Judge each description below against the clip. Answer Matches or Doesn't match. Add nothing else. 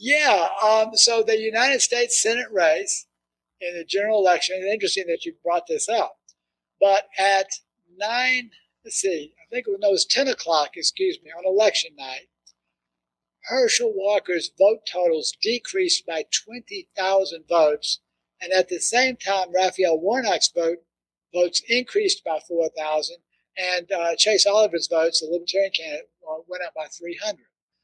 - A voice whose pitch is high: Matches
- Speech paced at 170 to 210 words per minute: Doesn't match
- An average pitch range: Doesn't match